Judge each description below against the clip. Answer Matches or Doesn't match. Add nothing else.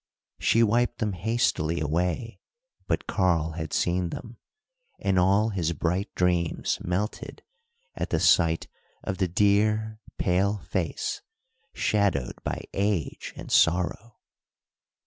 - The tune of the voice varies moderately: Matches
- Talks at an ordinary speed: Doesn't match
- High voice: Doesn't match